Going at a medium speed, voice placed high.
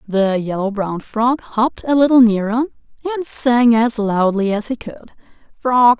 Yes: average, 160 wpm; high, 230 Hz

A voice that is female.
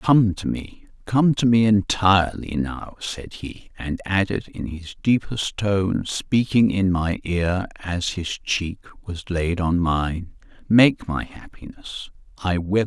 No: male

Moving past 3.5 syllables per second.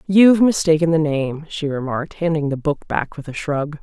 Yes: 5.2 syllables/s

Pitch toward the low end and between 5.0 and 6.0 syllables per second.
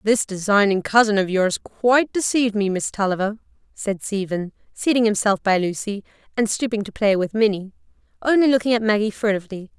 No: high, 210 Hz; 5.7 syllables/s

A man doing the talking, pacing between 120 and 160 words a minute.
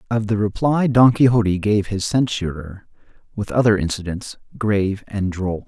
Yes: male; average, 150 wpm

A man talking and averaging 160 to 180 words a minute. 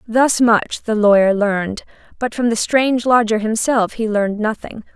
No: female; average, 170 wpm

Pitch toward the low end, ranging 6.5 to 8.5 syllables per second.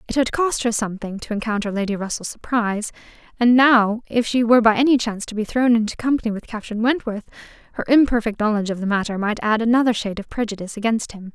No: high, 225 Hz; 6.7 syllables/s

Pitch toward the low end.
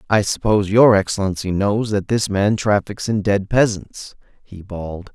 Yes: low, 100 Hz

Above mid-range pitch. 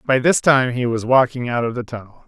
No: low, 125 Hz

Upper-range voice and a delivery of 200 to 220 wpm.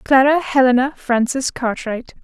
No: very high, 260 Hz; slow, 110 wpm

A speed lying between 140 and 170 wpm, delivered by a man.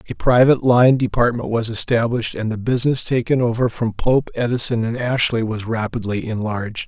Yes: average, 165 wpm; male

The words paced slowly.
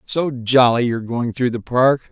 No: average, 200 wpm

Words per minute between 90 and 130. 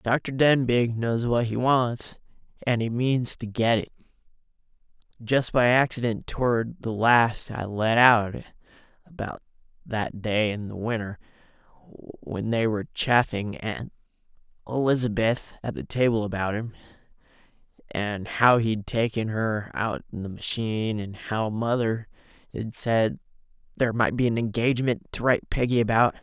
No: average, 140 wpm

